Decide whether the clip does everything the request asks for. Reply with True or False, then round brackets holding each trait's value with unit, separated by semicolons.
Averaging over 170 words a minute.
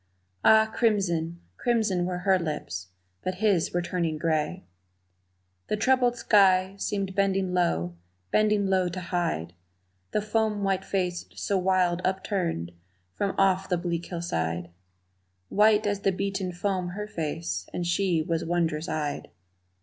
False (135 wpm)